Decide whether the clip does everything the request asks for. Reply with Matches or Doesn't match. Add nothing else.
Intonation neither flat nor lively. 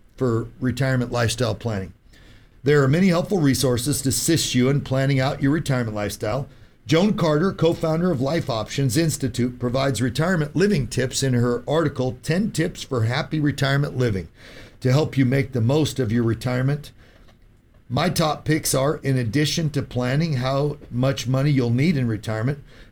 Matches